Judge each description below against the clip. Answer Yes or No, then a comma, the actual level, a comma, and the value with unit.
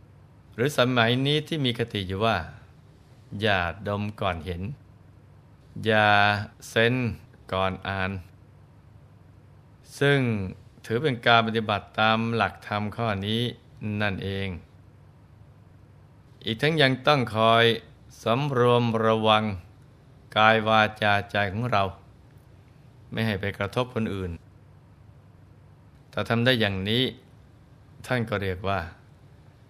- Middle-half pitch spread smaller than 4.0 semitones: Yes, average, 3.3 semitones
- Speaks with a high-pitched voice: No, low, 110 Hz